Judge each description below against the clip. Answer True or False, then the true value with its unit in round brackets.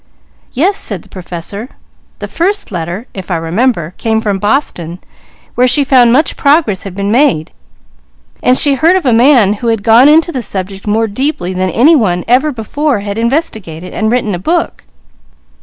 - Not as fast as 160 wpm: False (175 wpm)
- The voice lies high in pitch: True (225 Hz)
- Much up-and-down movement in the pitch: True (6.2 semitones)